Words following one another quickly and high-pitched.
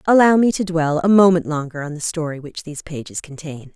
No: fast, 225 wpm; medium, 160 Hz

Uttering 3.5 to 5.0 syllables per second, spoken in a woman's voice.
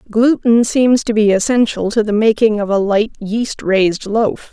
Yes: 4.5 syllables/s; female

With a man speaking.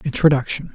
Yes: male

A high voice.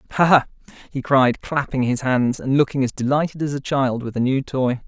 No: low, 135 Hz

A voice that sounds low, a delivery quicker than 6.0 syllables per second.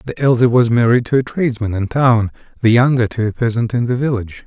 Yes: low, 120 Hz; 6.3 syllables/s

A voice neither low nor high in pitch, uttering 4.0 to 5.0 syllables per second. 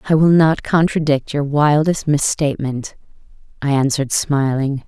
Yes: medium, 145 Hz; 4.7 syllables/s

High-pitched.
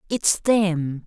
No: medium, 180 Hz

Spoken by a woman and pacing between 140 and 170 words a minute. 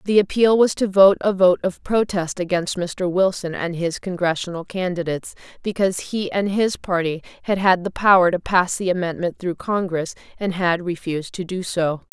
No: female; average, 185 wpm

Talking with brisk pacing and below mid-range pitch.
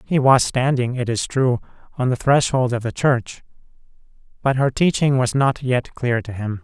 No: average, 190 wpm; low, 125 Hz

